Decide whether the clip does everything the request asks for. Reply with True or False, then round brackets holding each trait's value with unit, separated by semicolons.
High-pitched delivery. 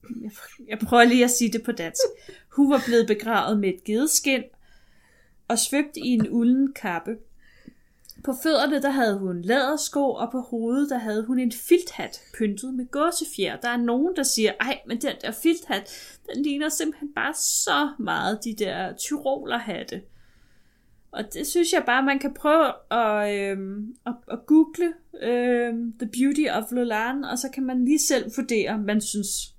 True (245 Hz)